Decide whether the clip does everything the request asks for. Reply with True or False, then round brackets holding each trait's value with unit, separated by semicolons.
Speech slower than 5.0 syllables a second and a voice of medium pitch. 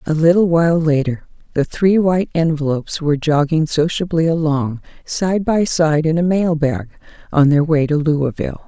False (5.1 syllables/s; 160 Hz)